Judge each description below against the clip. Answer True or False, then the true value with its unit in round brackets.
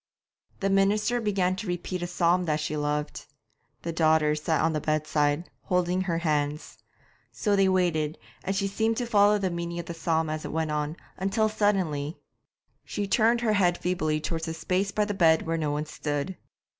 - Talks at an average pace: True (190 wpm)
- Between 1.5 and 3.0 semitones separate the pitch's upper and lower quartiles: False (4.1 semitones)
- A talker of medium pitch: True (170 Hz)